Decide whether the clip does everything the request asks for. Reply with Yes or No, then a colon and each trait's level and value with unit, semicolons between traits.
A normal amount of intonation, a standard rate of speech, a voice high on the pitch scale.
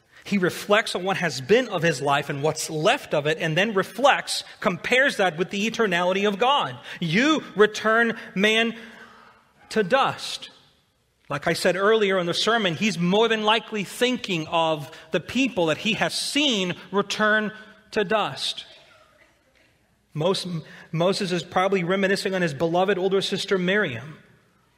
Yes: average, 4.0 semitones; average, 150 wpm; high, 195 Hz